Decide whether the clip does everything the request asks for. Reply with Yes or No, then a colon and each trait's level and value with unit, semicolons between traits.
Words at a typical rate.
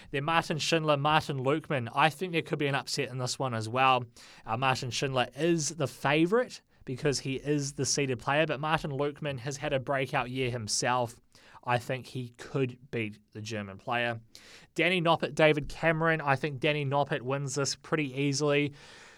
Yes: average, 180 wpm